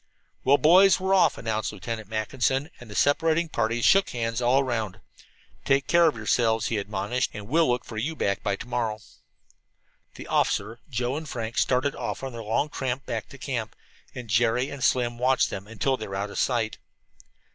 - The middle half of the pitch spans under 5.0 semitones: Yes, average, 3.6 semitones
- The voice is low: Yes, low, 120 Hz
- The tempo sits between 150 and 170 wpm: No, average, 190 wpm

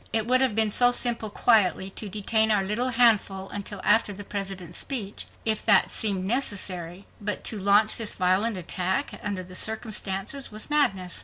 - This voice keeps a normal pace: Yes, average, 170 wpm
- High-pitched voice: Yes, high, 205 Hz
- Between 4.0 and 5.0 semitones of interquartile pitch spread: No, average, 2.8 semitones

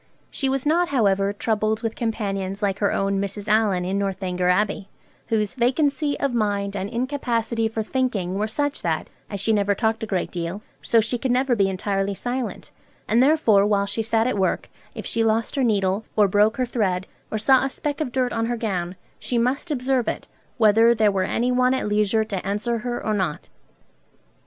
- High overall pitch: Yes, high, 220 Hz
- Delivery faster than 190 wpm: Yes, average, 200 wpm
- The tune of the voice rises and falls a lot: No, average, 3.7 semitones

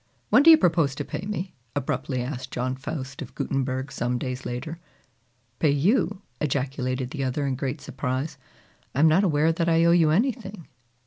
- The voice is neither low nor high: Yes, medium, 145 Hz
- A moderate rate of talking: Yes, average, 180 wpm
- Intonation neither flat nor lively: Yes, average, 4.4 semitones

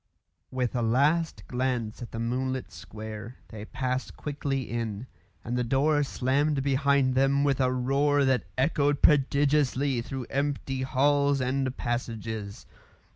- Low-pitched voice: Yes, low, 130 Hz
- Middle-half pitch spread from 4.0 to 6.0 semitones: No, narrow, 2.5 semitones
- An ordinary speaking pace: No, slow, 130 wpm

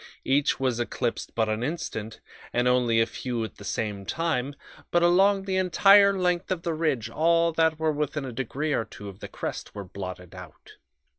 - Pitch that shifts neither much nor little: No, wide, 7.0 semitones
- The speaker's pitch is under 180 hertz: Yes, low, 135 Hz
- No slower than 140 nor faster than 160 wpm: No, average, 195 wpm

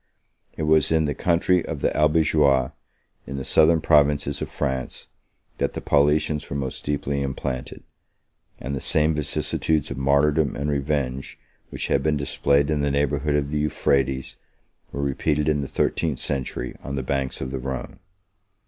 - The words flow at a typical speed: Yes, average, 165 wpm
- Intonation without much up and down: Yes, narrow, 1.9 semitones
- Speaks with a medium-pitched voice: No, very low, 70 Hz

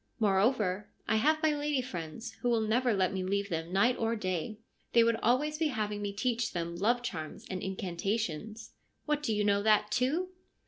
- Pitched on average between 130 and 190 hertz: No, high, 215 Hz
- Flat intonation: No, average, 4.2 semitones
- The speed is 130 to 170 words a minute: No, average, 195 wpm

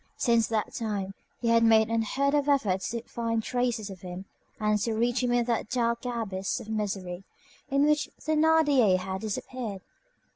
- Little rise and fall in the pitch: No, average, 3.2 semitones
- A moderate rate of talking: Yes, average, 170 wpm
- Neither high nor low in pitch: No, high, 230 Hz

